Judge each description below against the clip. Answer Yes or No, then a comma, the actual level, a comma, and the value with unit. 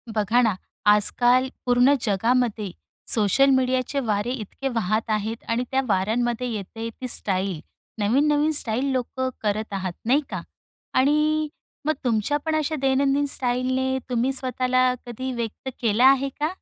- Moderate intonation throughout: Yes, average, 3.4 semitones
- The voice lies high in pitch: Yes, high, 245 Hz